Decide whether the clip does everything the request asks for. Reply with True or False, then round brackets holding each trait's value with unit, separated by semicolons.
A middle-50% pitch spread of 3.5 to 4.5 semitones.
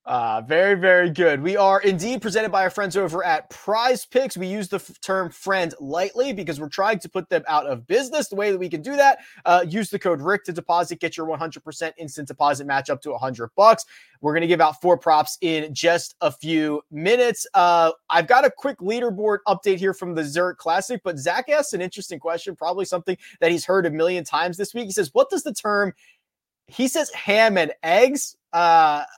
True (4.1 semitones)